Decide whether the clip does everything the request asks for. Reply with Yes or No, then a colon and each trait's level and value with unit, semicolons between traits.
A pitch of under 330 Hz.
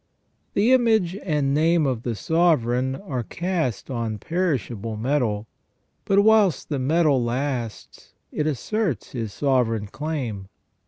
Yes: medium, 140 Hz